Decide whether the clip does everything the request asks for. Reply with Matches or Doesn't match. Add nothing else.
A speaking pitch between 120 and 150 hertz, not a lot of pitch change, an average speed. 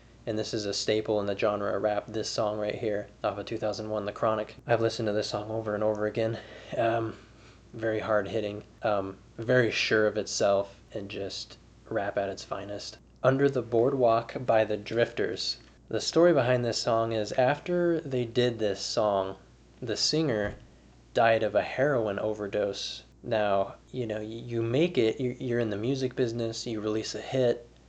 Doesn't match